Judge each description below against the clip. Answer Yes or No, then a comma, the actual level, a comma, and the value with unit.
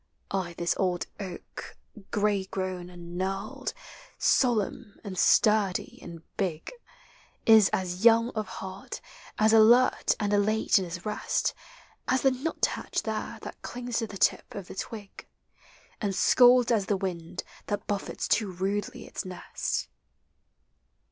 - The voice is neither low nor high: No, high, 200 Hz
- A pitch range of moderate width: Yes, average, 3.0 semitones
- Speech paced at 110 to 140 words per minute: Yes, slow, 135 wpm